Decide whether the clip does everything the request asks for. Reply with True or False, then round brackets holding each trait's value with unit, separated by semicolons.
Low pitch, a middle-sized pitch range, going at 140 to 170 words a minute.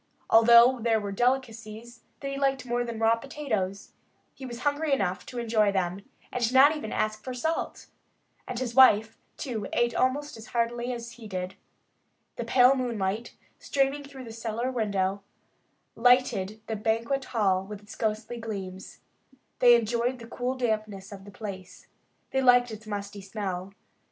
False (230 Hz; 3.2 semitones; 160 wpm)